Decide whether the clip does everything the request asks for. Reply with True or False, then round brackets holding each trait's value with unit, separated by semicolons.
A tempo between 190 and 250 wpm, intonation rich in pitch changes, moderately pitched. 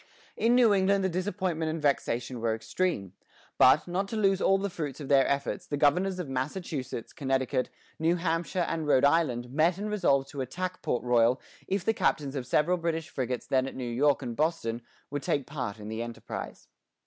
True (195 wpm; 5.7 semitones; 150 Hz)